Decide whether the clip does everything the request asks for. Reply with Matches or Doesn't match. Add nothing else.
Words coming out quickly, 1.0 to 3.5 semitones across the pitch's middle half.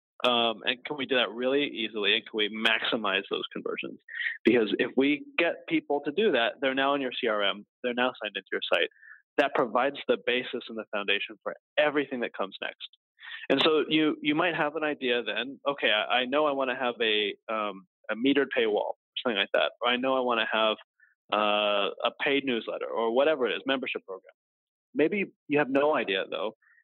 Doesn't match